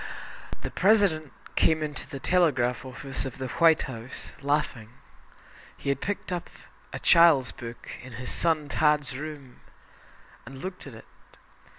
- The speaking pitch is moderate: Yes, medium, 145 Hz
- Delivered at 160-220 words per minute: No, average, 145 wpm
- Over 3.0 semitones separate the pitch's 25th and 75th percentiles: Yes, average, 3.9 semitones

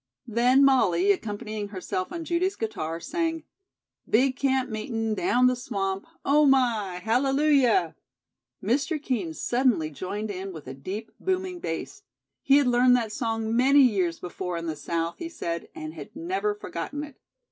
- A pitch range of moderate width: No, wide, 6.5 semitones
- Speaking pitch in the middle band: No, high, 235 Hz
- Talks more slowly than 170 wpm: Yes, average, 155 wpm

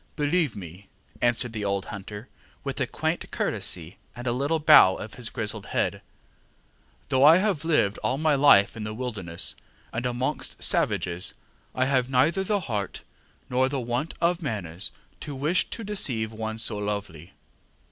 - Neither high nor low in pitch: No, low, 120 Hz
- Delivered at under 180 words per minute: Yes, average, 160 wpm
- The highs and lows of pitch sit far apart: Yes, wide, 6.0 semitones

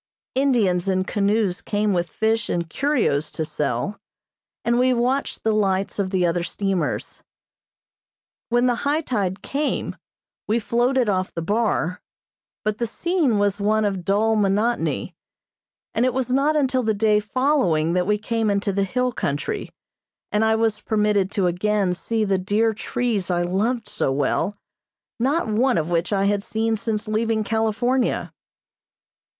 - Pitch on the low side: No, high, 215 Hz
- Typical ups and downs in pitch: Yes, average, 3.7 semitones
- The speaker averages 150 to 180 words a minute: Yes, average, 155 wpm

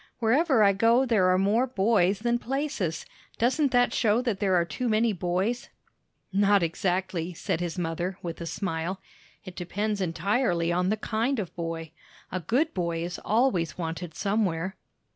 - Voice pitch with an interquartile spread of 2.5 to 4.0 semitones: No, average, 4.7 semitones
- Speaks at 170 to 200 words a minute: No, average, 160 wpm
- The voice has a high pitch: Yes, high, 195 Hz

